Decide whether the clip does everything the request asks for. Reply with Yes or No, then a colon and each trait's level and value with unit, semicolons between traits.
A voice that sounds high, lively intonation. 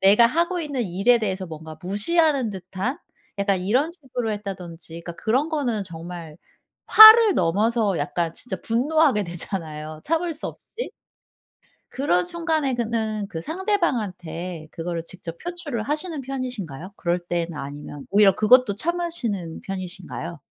Yes: high, 205 Hz; wide, 7.9 semitones